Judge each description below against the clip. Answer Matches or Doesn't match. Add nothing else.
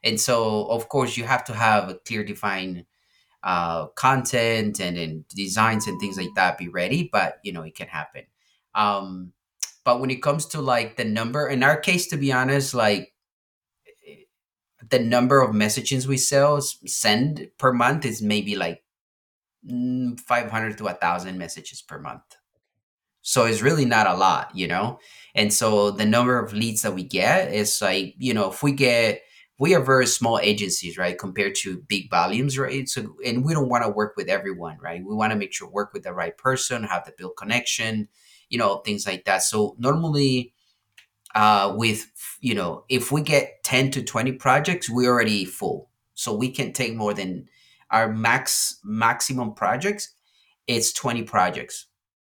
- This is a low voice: Matches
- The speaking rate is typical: Matches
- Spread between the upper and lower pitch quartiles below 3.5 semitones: Doesn't match